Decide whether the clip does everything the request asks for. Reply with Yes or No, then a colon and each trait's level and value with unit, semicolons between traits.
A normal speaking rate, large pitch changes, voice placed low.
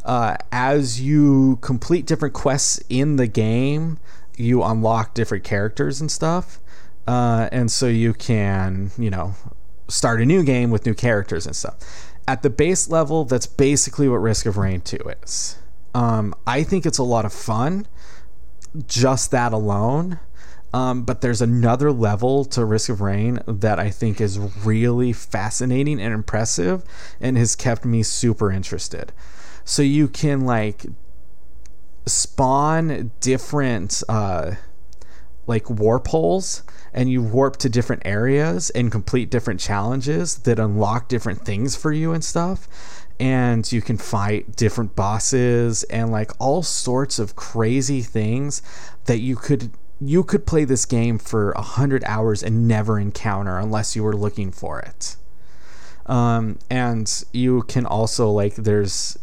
No: average, 150 wpm; average, 3.8 semitones; low, 115 Hz